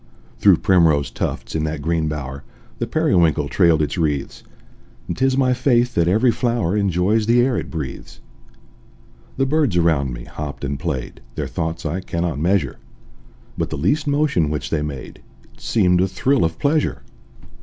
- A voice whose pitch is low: Yes, very low, 85 Hz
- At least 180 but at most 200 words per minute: No, average, 165 wpm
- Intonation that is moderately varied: No, wide, 7.6 semitones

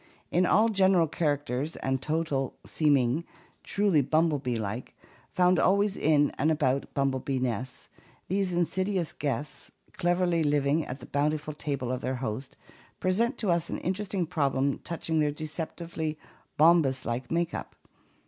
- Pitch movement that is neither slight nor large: Yes, average, 4.4 semitones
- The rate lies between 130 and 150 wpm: Yes, average, 140 wpm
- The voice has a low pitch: No, medium, 155 Hz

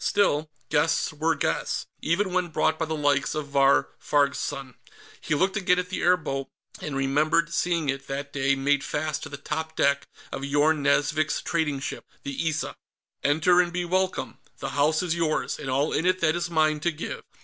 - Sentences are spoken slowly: No, average, 195 wpm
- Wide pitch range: No, average, 3.0 semitones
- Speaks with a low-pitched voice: No, medium, 155 Hz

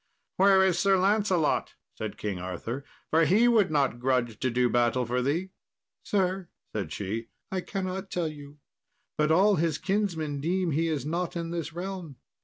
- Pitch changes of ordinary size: No, wide, 6.4 semitones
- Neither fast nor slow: Yes, average, 170 wpm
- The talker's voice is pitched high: No, medium, 165 Hz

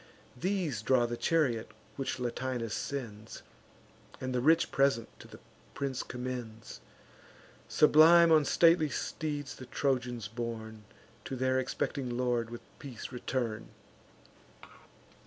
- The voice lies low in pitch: Yes, low, 125 Hz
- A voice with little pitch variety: No, average, 3.2 semitones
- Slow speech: Yes, slow, 115 wpm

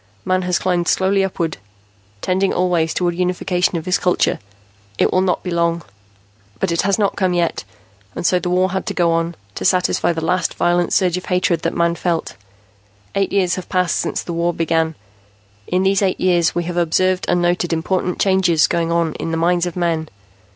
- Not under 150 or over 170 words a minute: No, average, 200 wpm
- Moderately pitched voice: Yes, medium, 175 Hz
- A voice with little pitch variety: Yes, narrow, 1.5 semitones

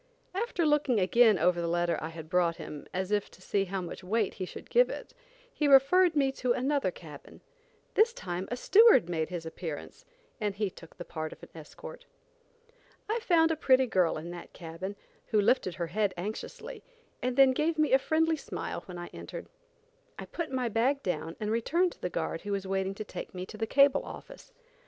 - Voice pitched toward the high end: Yes, high, 210 Hz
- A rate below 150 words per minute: No, fast, 205 wpm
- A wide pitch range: Yes, wide, 7.9 semitones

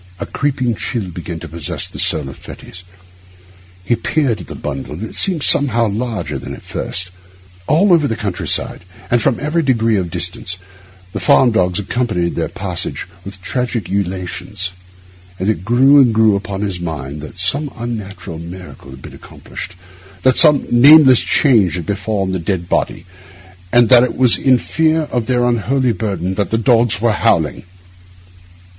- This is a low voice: Yes, low, 105 Hz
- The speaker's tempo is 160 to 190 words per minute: Yes, average, 170 wpm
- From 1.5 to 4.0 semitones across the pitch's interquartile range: No, wide, 5.5 semitones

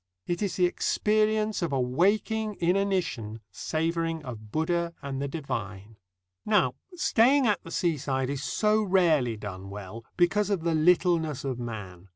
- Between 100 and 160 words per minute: Yes, average, 150 wpm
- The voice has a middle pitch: Yes, medium, 165 Hz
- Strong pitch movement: Yes, wide, 7.8 semitones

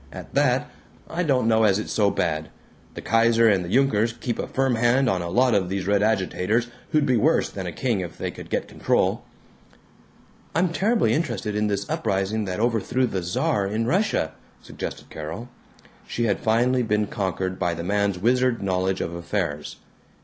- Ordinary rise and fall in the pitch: Yes, average, 4.3 semitones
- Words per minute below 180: No, average, 185 wpm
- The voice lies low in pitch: Yes, low, 105 Hz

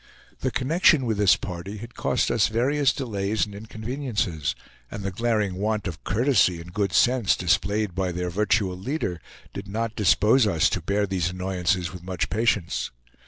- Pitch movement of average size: Yes, average, 3.9 semitones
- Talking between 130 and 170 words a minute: Yes, average, 165 wpm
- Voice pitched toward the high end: No, low, 100 Hz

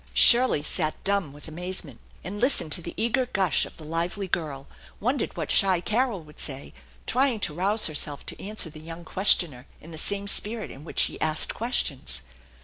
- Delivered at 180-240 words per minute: Yes, average, 185 wpm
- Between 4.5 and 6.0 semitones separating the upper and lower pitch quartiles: Yes, wide, 5.4 semitones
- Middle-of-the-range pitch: Yes, medium, 175 Hz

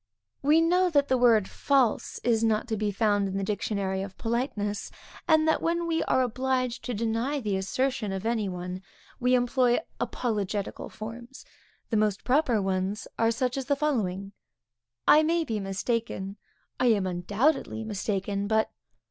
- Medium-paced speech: Yes, average, 160 wpm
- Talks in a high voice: Yes, high, 225 Hz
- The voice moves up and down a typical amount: Yes, average, 4.4 semitones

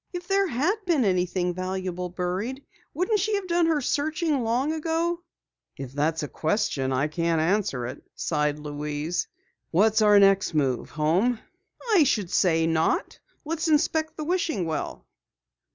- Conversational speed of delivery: Yes, average, 150 wpm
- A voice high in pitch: Yes, high, 195 Hz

